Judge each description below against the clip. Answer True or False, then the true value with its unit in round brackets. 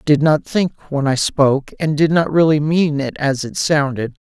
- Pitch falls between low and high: True (145 Hz)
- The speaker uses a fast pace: True (225 wpm)